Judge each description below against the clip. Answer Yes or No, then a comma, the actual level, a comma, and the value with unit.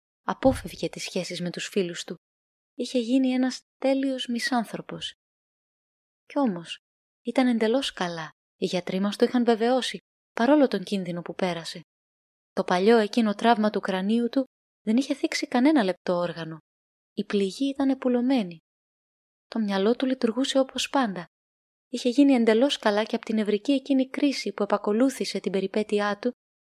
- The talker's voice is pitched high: Yes, high, 225 Hz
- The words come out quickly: No, average, 150 wpm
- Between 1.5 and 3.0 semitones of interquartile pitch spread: No, average, 5.3 semitones